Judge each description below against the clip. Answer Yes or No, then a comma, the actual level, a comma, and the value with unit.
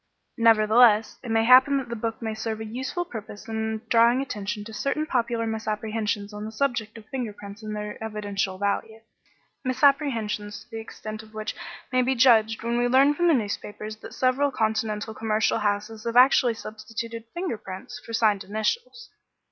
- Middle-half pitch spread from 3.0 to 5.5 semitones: No, narrow, 2.4 semitones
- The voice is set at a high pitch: Yes, high, 220 Hz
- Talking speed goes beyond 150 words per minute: Yes, average, 170 wpm